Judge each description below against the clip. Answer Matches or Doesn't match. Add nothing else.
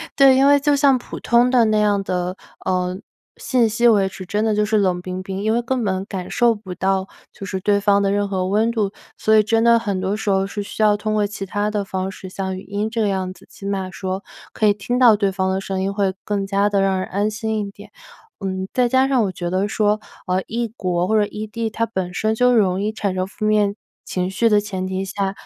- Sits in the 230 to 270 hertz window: Doesn't match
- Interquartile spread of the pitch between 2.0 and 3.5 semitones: Matches